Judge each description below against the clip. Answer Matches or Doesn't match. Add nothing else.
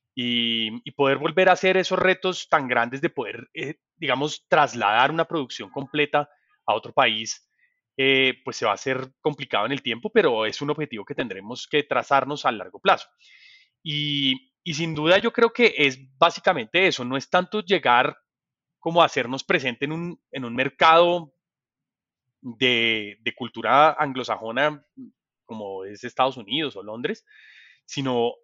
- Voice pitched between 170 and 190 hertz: Doesn't match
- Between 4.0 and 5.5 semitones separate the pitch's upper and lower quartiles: Matches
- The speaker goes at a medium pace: Matches